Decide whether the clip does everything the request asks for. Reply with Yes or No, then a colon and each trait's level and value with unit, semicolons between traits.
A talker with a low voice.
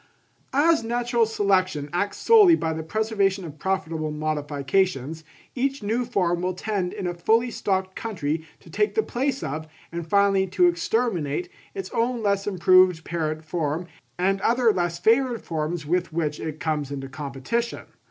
No: medium, 185 Hz